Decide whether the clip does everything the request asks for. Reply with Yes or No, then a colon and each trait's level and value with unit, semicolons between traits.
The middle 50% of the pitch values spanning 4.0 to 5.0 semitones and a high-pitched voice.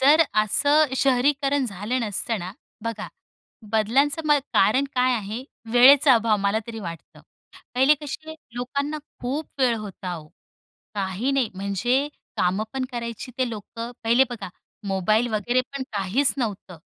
Yes: average, 4.5 semitones; high, 240 Hz